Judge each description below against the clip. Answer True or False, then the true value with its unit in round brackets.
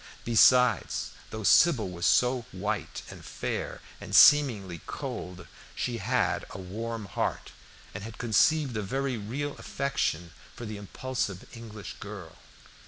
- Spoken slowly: True (130 wpm)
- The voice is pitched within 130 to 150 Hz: False (110 Hz)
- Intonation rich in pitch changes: False (4.3 semitones)